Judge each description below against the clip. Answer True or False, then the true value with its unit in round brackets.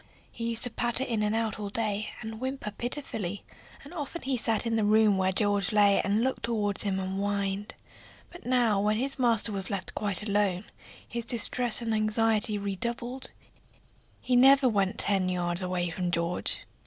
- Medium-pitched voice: False (215 Hz)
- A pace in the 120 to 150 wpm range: False (180 wpm)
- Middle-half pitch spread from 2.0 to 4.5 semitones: True (2.9 semitones)